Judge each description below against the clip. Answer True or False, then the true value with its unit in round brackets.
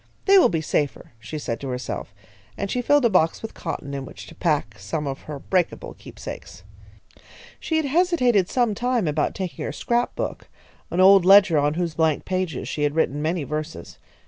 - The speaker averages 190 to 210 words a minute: True (195 wpm)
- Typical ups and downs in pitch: False (6.4 semitones)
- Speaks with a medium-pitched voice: True (165 Hz)